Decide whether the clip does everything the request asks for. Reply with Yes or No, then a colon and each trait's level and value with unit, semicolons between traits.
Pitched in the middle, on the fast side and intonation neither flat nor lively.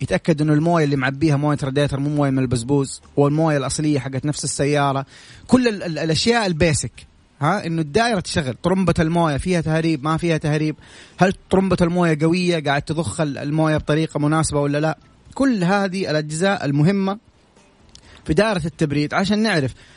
Yes: medium, 155 Hz; fast, 155 wpm; average, 3.5 semitones